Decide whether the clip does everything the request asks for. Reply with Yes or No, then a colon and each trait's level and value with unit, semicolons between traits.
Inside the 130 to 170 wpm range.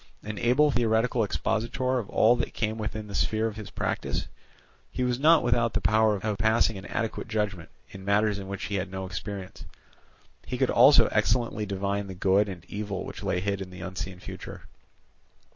No: average, 190 wpm